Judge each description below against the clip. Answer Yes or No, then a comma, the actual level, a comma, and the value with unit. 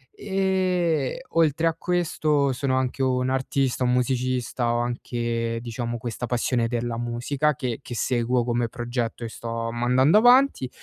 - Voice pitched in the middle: No, low, 125 Hz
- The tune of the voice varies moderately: Yes, average, 3.6 semitones